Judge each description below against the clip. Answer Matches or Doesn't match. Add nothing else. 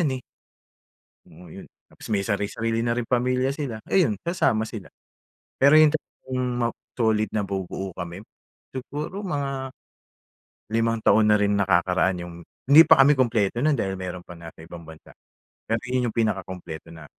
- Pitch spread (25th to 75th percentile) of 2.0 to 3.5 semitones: Doesn't match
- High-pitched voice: Doesn't match